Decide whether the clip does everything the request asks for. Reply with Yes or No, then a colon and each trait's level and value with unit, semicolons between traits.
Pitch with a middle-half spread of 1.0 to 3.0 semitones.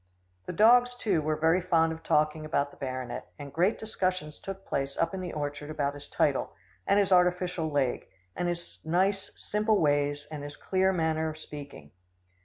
No: average, 4.1 semitones